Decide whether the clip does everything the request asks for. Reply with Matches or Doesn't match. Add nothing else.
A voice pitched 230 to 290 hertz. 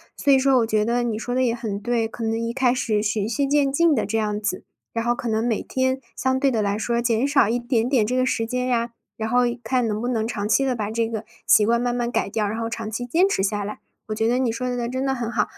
Matches